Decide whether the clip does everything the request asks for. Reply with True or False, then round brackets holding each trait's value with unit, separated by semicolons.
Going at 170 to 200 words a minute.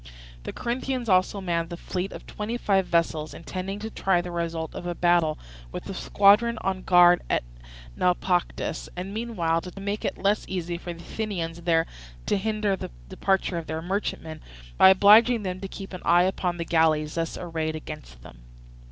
True (180 wpm)